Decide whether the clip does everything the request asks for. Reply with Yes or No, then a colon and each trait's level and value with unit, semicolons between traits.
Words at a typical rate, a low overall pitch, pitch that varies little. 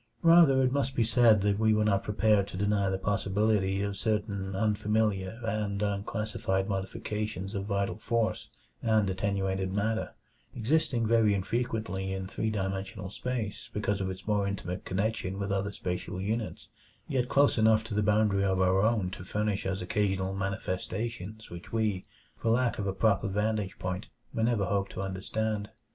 Yes: average, 165 wpm; low, 105 Hz; narrow, 2.3 semitones